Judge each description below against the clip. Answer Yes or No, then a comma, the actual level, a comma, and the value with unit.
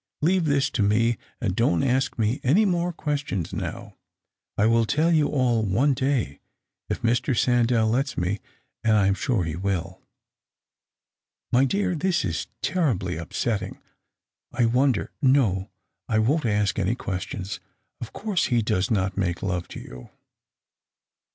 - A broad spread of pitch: Yes, wide, 6.0 semitones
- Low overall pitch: Yes, low, 115 Hz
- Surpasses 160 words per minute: No, average, 150 wpm